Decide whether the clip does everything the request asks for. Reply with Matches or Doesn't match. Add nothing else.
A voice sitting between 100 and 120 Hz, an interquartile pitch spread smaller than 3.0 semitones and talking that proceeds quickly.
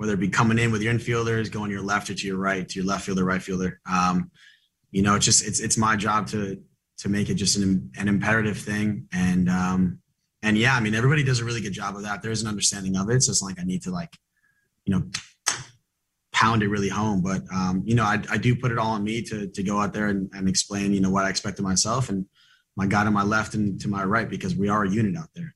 Matches